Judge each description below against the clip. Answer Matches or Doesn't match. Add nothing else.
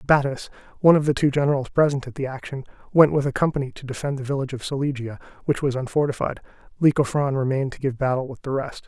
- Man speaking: Matches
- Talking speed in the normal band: Doesn't match